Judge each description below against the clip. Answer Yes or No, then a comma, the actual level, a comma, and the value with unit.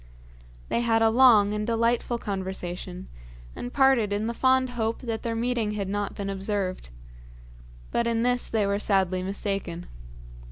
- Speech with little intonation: No, average, 3.0 semitones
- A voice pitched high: Yes, high, 215 Hz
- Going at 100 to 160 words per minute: Yes, average, 155 wpm